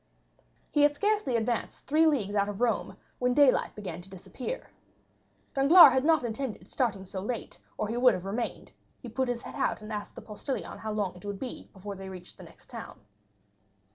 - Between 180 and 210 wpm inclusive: Yes, average, 200 wpm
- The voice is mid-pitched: No, high, 230 Hz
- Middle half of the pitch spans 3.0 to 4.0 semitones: No, average, 4.7 semitones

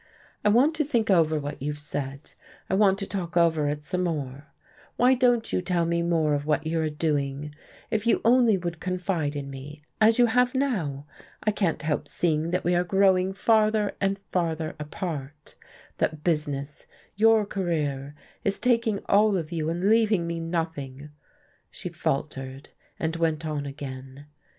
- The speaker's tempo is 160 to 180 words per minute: Yes, average, 170 wpm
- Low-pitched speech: No, medium, 165 Hz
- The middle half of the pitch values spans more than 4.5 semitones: Yes, average, 5.0 semitones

